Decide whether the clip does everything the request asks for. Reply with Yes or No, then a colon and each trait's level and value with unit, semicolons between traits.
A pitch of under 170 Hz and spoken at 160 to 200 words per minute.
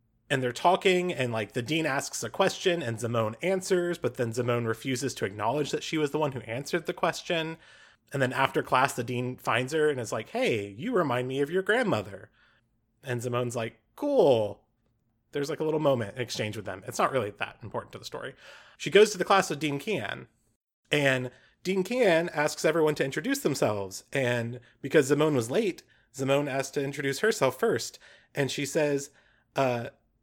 Yes: medium, 140 Hz; average, 195 wpm